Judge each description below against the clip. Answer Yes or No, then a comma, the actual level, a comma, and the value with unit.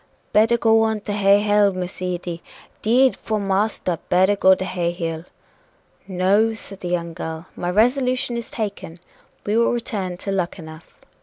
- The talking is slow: No, average, 160 wpm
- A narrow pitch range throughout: No, average, 3.7 semitones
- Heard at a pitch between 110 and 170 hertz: No, high, 195 Hz